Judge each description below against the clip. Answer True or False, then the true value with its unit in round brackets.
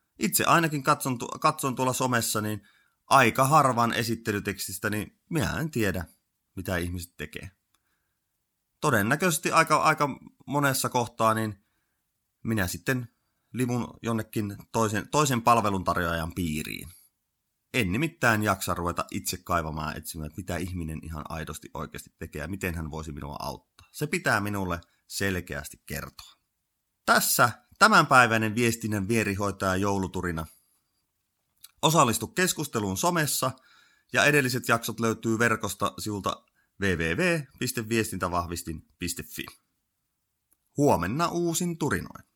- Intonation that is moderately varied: False (6.1 semitones)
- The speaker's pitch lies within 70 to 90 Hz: False (110 Hz)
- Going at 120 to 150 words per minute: False (105 wpm)